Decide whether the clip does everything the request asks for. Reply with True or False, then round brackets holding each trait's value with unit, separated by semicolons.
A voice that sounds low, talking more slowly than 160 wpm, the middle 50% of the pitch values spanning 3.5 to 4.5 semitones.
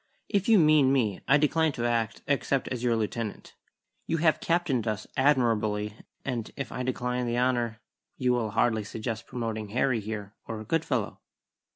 False (120 Hz; 165 wpm; 3.8 semitones)